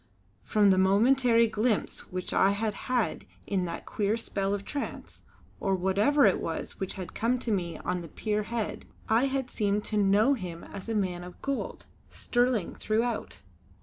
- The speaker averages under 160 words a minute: No, average, 175 wpm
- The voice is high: Yes, high, 210 Hz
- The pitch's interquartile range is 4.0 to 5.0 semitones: No, average, 3.5 semitones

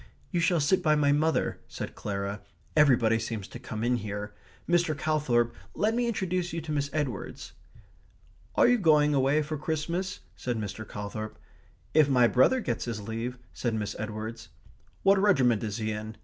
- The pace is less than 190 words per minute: Yes, average, 170 wpm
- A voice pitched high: No, low, 130 Hz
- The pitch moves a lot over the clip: Yes, wide, 6.3 semitones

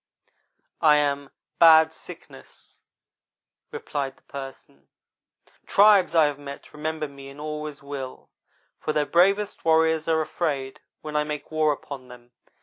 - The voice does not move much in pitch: Yes, narrow, 2.3 semitones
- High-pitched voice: No, medium, 150 Hz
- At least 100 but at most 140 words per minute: Yes, slow, 135 wpm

